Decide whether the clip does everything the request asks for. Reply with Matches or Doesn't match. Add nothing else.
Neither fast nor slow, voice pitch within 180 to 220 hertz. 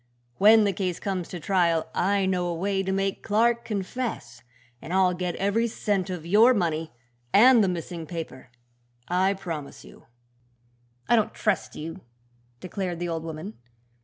Matches